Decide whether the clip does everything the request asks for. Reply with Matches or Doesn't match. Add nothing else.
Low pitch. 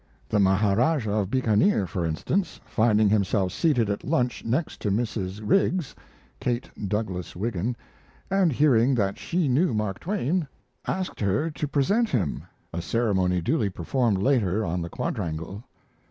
Matches